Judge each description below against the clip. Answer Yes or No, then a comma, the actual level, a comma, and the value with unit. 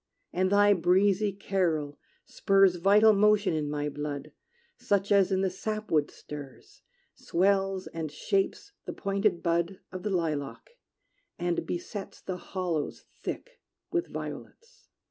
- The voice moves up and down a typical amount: Yes, average, 3.5 semitones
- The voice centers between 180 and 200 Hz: Yes, high, 190 Hz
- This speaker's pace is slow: Yes, slow, 125 wpm